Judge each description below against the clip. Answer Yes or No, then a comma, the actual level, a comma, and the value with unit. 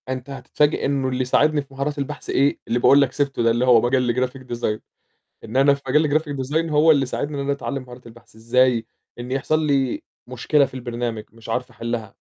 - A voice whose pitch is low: Yes, low, 130 Hz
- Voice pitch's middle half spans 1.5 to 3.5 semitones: Yes, average, 2.7 semitones